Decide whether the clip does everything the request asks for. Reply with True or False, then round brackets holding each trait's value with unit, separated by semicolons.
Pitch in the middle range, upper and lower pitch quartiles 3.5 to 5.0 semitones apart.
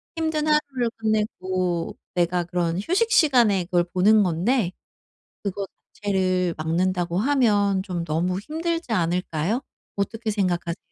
False (195 Hz; 4.7 semitones)